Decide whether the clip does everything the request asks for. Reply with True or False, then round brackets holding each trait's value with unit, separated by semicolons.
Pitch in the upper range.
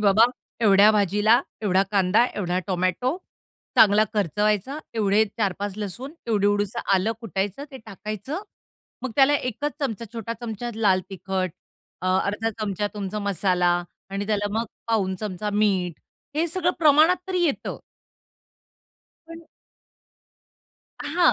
True (210 Hz)